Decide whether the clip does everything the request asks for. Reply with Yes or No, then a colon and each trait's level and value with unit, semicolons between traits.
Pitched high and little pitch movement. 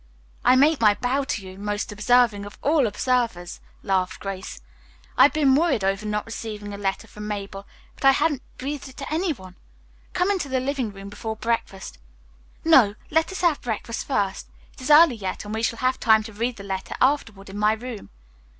No: high, 225 Hz; average, 5.0 semitones